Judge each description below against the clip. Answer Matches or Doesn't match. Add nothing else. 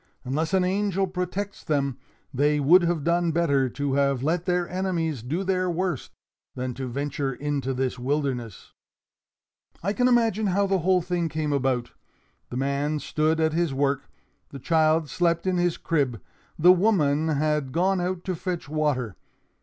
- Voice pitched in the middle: Matches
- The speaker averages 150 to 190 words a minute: Matches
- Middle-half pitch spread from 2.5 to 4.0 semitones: Doesn't match